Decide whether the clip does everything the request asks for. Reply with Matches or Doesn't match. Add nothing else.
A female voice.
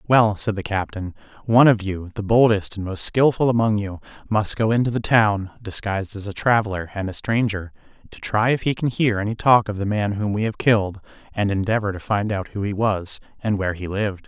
Doesn't match